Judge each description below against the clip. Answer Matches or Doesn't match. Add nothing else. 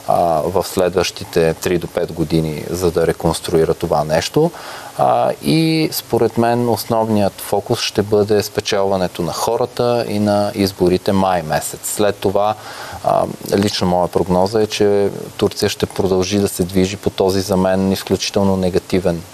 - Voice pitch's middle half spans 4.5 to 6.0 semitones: Doesn't match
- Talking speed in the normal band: Matches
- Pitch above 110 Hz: Doesn't match